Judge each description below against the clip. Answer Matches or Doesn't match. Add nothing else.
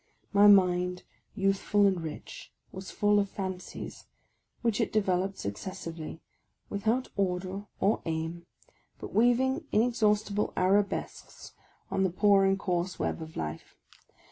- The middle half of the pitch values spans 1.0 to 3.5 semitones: Matches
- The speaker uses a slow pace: Matches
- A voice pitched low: Doesn't match